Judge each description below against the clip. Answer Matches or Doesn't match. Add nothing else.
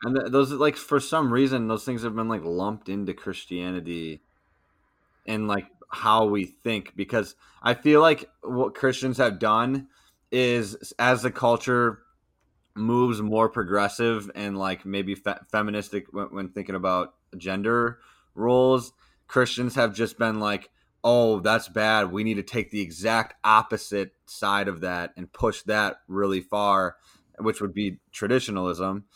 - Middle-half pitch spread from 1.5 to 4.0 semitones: Matches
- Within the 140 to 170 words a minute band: Matches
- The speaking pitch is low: Matches